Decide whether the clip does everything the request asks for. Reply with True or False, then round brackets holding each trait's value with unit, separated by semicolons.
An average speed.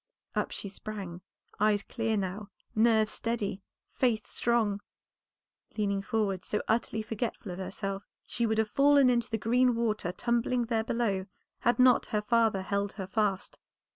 True (150 wpm)